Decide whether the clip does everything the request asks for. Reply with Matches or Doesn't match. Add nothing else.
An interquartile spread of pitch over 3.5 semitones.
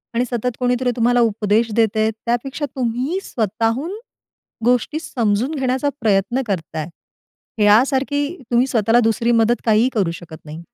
Doesn't match